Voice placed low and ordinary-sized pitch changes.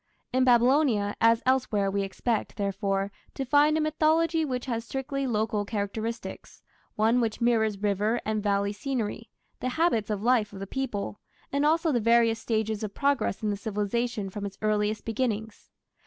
No: high, 225 Hz; average, 3.7 semitones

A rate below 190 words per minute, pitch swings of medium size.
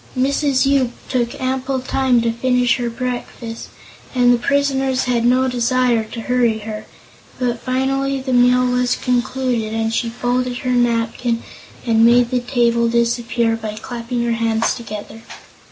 No: average, 150 wpm; narrow, 1.6 semitones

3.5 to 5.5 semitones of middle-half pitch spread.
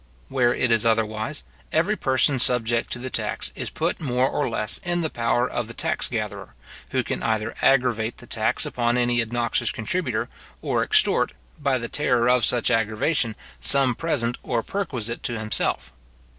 No: narrow, 2.6 semitones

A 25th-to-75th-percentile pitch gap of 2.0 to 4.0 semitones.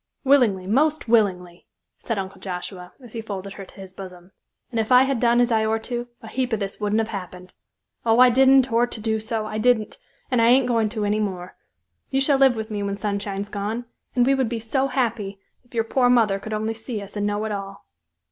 Yes: average, 3.3 semitones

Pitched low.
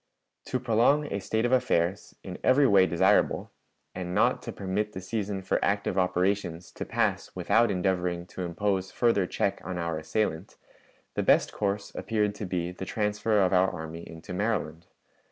Yes: very low, 95 Hz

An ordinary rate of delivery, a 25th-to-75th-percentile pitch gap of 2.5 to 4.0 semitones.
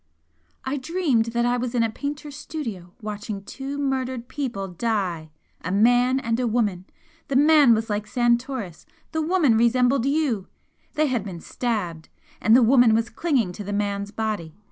No: average, 165 wpm; average, 4.5 semitones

